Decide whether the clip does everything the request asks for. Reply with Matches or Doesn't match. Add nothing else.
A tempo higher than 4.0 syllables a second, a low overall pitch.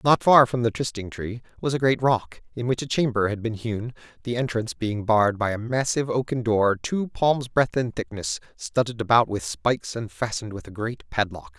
Matches